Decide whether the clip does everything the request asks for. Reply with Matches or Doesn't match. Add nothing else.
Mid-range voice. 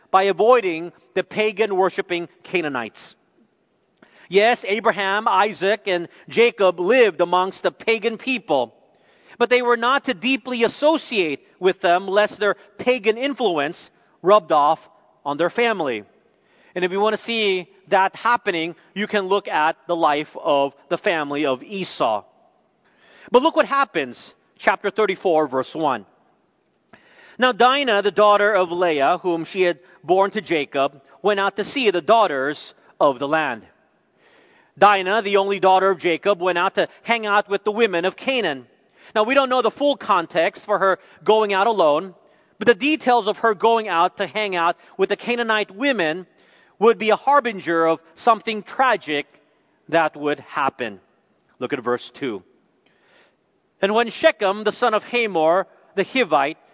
Doesn't match